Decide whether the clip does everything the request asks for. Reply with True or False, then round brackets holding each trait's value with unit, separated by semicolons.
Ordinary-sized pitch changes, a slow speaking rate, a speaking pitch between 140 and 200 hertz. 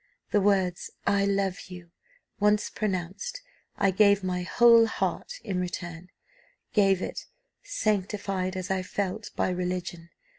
False (2.2 semitones; 125 wpm; 190 Hz)